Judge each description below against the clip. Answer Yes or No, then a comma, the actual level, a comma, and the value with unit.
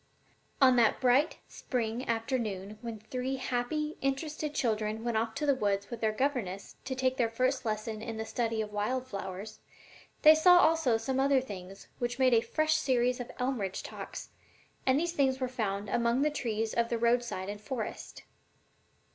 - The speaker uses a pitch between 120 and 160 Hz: No, high, 240 Hz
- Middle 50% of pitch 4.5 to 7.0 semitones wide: No, average, 3.3 semitones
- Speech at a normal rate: Yes, average, 180 wpm